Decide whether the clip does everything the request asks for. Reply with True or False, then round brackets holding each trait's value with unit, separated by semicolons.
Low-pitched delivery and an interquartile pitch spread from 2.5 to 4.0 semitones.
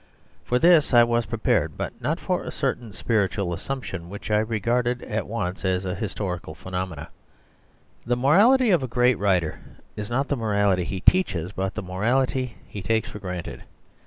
False (105 Hz; 4.8 semitones)